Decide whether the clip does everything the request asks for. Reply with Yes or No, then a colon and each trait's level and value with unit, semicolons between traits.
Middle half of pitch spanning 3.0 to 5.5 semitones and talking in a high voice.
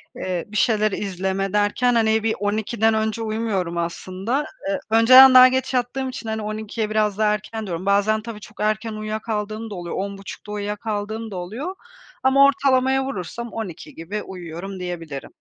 No: narrow, 2.6 semitones; high, 215 Hz